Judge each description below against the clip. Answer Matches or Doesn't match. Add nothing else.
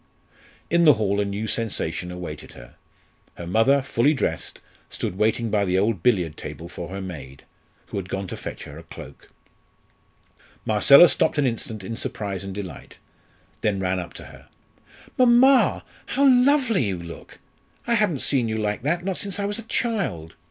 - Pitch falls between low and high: Doesn't match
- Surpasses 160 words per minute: Matches